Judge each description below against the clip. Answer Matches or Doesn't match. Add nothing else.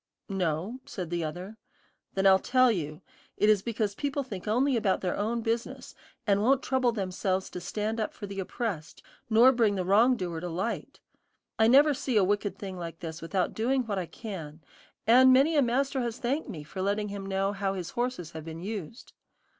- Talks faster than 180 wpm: Matches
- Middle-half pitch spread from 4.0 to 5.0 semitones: Matches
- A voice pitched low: Doesn't match